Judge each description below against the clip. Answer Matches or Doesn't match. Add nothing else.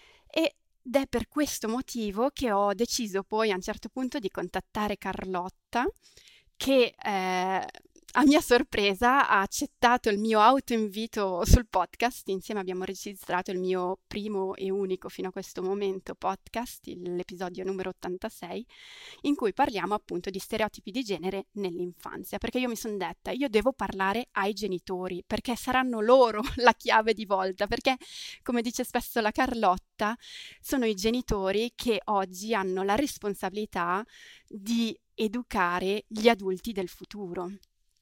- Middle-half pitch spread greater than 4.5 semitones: Doesn't match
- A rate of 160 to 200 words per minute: Doesn't match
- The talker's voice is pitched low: Doesn't match